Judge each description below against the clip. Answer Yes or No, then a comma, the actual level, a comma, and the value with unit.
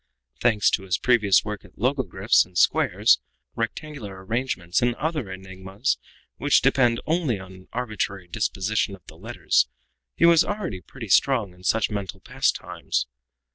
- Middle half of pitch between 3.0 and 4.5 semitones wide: No, average, 4.9 semitones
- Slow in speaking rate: No, average, 145 wpm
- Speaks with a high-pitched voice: No, low, 105 Hz